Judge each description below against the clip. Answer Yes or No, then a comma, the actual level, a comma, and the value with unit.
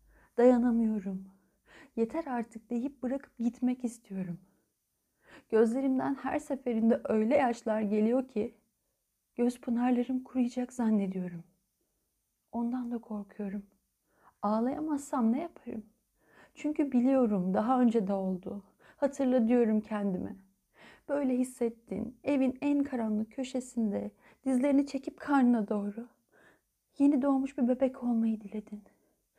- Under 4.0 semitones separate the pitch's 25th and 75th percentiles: Yes, average, 3.6 semitones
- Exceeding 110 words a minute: No, average, 100 wpm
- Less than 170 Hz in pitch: No, high, 240 Hz